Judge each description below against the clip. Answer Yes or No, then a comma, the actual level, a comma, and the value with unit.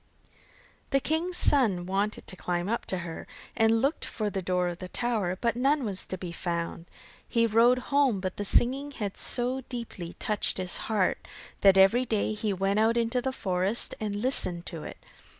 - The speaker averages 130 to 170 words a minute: No, average, 185 wpm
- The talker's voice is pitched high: Yes, high, 210 Hz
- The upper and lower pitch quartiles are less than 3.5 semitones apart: No, average, 4.7 semitones